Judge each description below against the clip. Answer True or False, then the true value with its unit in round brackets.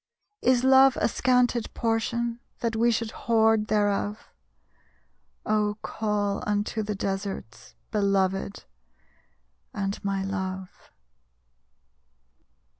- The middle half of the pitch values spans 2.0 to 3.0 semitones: True (2.6 semitones)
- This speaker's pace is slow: True (95 wpm)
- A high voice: True (210 Hz)